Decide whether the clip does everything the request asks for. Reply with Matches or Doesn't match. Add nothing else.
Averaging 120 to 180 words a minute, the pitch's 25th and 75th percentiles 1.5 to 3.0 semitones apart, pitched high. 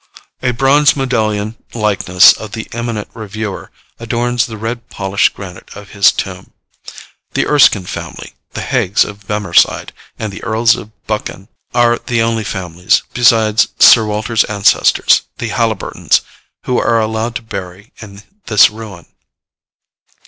Doesn't match